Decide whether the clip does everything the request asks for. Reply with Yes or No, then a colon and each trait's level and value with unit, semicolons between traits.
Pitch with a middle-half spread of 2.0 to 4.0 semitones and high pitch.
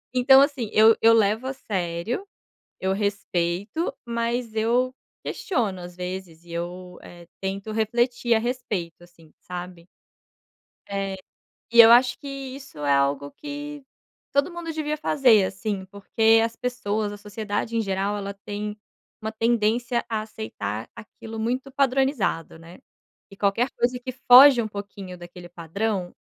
No: average, 4.6 semitones; high, 220 Hz